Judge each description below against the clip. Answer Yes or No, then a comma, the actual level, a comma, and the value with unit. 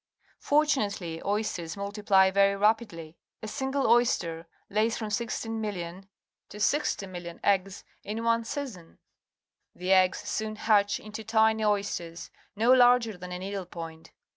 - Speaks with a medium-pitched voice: No, high, 205 Hz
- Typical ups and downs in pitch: Yes, average, 3.5 semitones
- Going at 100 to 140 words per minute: Yes, slow, 135 wpm